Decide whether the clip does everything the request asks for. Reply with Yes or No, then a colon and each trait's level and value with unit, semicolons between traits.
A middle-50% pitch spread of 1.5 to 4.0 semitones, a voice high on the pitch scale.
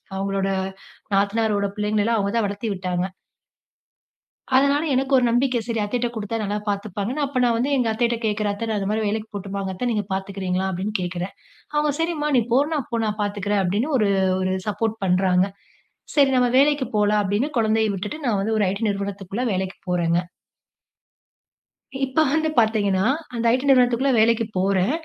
Yes: average, 3.7 semitones; high, 210 Hz